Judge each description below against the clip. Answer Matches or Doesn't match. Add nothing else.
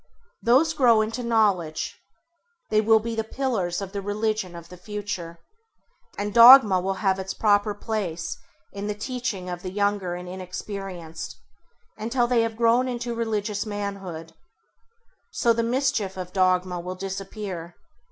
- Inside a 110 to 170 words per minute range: Matches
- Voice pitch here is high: Matches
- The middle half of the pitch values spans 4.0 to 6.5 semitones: Doesn't match